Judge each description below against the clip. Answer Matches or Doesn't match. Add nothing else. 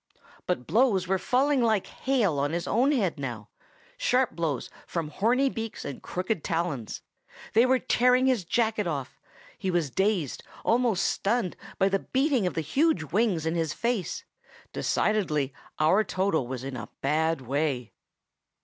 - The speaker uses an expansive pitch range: Matches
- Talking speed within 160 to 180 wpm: Doesn't match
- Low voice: Doesn't match